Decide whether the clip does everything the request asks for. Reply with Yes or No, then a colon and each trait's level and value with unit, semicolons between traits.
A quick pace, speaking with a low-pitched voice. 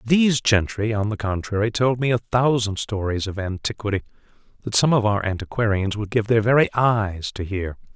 No: average, 180 wpm; low, 110 Hz